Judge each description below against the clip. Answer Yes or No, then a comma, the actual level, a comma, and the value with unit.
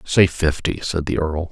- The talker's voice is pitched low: Yes, very low, 80 Hz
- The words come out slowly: No, average, 200 wpm